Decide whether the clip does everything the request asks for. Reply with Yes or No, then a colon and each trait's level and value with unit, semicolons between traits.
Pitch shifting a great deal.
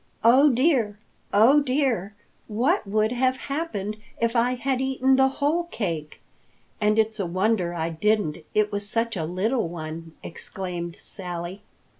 Yes: wide, 6.1 semitones